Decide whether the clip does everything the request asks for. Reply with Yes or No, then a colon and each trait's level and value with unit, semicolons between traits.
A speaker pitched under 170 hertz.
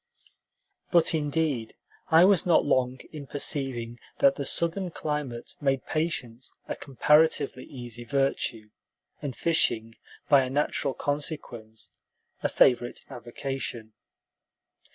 Yes: low, 135 Hz